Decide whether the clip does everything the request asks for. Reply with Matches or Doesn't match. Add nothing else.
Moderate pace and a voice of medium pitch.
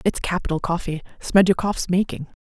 Doesn't match